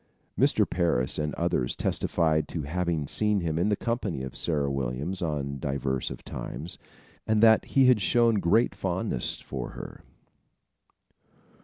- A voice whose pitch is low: Yes, very low, 80 Hz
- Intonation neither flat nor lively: No, wide, 6.9 semitones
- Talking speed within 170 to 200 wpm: No, average, 145 wpm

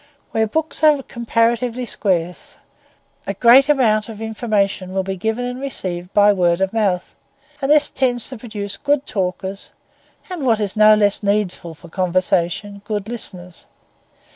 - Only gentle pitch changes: No, average, 4.2 semitones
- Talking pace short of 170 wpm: Yes, average, 150 wpm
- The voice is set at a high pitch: Yes, high, 215 Hz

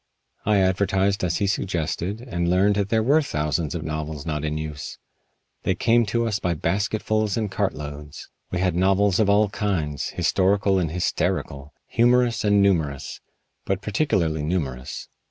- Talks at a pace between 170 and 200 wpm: No, average, 155 wpm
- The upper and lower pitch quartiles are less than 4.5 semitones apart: No, average, 4.8 semitones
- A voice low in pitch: Yes, very low, 95 Hz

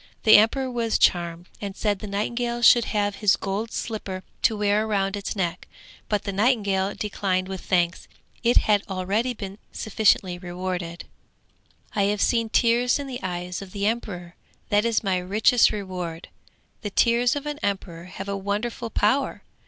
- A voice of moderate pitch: No, high, 205 Hz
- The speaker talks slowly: No, average, 165 wpm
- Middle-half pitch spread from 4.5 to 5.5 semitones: No, average, 3.3 semitones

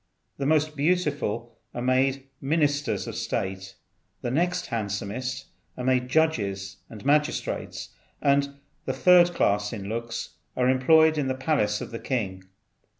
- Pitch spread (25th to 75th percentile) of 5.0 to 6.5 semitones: Yes, average, 5.3 semitones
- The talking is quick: No, average, 140 wpm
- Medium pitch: No, low, 130 Hz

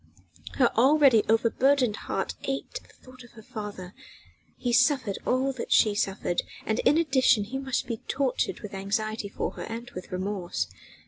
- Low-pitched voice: No, high, 230 Hz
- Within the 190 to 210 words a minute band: No, average, 160 wpm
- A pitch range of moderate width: Yes, average, 4.1 semitones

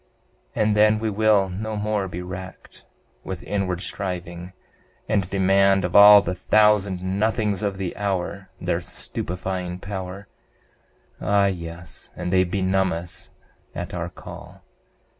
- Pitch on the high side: No, very low, 95 Hz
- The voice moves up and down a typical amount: No, narrow, 2.1 semitones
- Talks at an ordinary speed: No, slow, 130 wpm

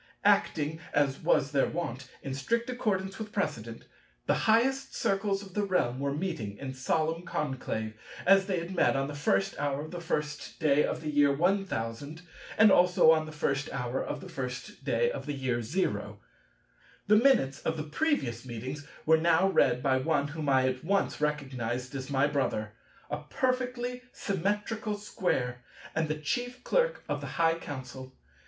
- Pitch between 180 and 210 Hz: No, medium, 150 Hz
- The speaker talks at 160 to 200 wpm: Yes, average, 175 wpm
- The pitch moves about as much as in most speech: No, wide, 6.5 semitones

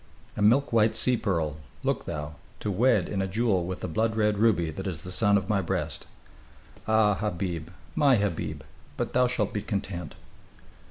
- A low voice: Yes, low, 100 Hz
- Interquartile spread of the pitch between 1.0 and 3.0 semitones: No, average, 4.1 semitones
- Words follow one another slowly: No, average, 180 wpm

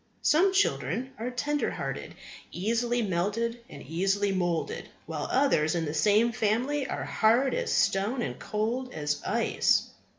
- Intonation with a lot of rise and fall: Yes, wide, 5.9 semitones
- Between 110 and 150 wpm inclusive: Yes, average, 140 wpm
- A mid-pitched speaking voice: No, high, 220 Hz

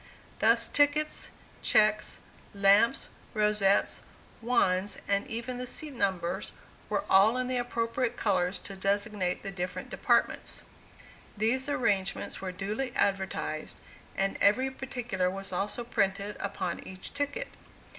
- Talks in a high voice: Yes, high, 210 Hz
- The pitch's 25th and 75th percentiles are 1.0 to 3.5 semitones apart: No, average, 4.1 semitones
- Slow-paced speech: Yes, slow, 120 wpm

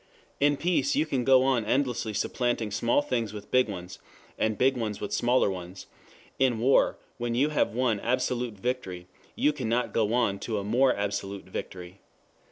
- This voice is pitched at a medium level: No, low, 120 Hz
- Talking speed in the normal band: Yes, average, 175 wpm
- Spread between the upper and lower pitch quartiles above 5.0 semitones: No, average, 3.9 semitones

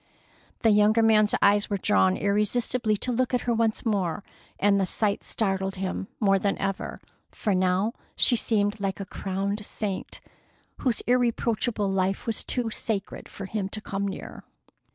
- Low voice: No, high, 205 Hz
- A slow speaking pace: No, average, 160 wpm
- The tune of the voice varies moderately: No, narrow, 2.3 semitones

